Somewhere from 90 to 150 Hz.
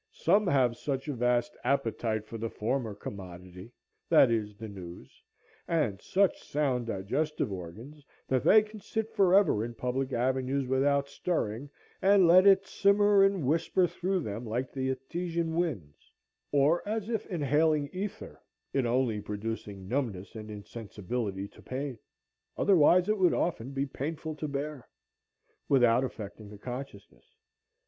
Yes: low, 135 Hz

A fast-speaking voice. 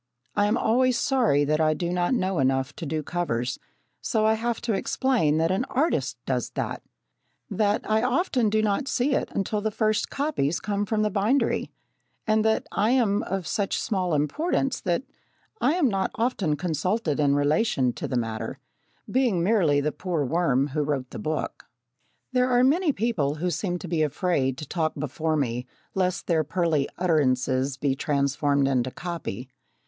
No: average, 175 wpm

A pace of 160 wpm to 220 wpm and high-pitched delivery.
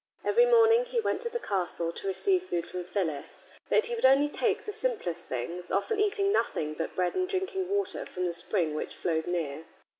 Yes: fast, 205 wpm; high, 235 Hz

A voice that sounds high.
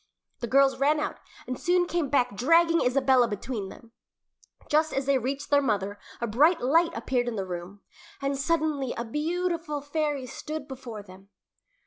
Yes: very high, 270 Hz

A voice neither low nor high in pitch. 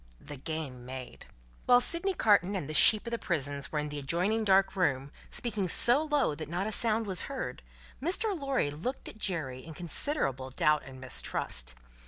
Yes: medium, 175 Hz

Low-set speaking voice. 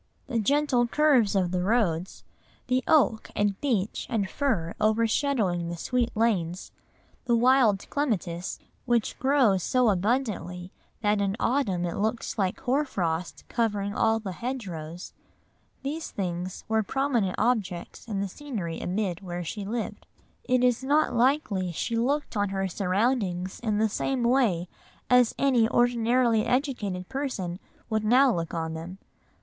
No: high, 220 Hz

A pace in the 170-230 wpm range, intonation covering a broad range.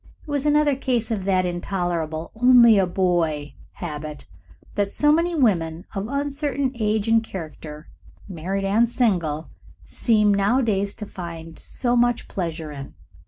No: average, 140 wpm; wide, 6.2 semitones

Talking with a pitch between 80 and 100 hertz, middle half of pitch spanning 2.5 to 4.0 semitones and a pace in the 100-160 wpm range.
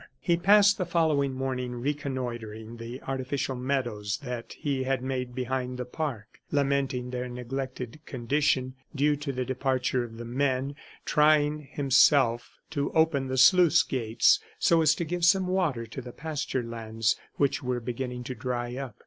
No: low, 130 Hz; average, 2.8 semitones; average, 155 wpm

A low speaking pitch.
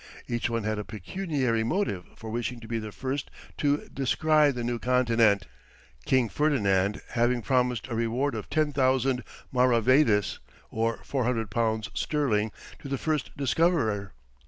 Yes: low, 120 Hz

